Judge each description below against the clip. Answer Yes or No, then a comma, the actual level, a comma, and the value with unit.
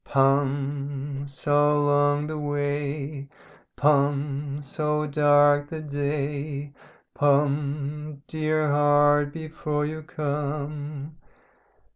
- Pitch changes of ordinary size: No, narrow, 0.9 semitones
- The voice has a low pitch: No, medium, 145 Hz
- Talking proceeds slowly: Yes, slow, 80 wpm